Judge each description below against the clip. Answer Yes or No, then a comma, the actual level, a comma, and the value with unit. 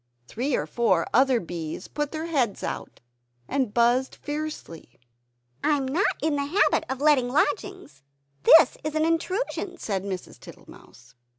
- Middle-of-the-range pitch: No, very high, 275 Hz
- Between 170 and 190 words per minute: No, average, 150 wpm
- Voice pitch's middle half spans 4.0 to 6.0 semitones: Yes, average, 5.1 semitones